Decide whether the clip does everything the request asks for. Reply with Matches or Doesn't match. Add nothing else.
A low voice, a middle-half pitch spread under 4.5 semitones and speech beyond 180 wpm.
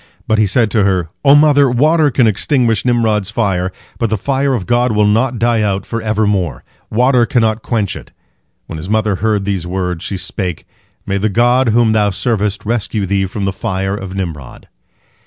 Matches